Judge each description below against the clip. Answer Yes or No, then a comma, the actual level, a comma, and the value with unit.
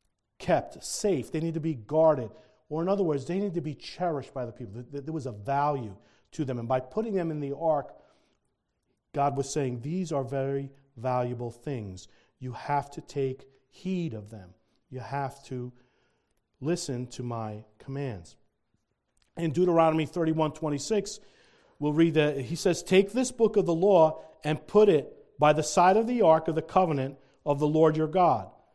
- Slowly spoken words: No, average, 180 wpm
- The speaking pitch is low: No, medium, 150 Hz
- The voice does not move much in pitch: No, average, 4.1 semitones